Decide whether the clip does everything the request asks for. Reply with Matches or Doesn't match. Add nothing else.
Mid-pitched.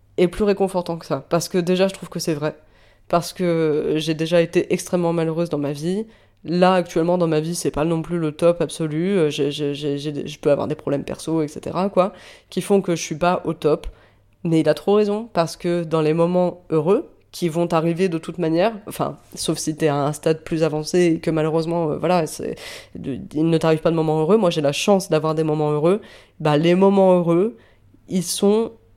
Matches